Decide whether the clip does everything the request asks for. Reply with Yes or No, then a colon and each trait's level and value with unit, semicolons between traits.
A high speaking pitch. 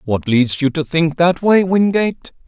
No: medium, 160 Hz